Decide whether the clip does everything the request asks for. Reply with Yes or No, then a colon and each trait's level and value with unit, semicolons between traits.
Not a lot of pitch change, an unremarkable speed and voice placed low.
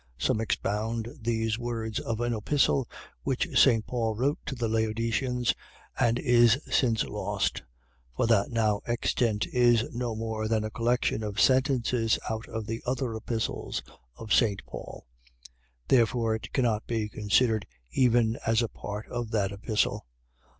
Yes: narrow, 1.7 semitones; average, 145 wpm; low, 115 Hz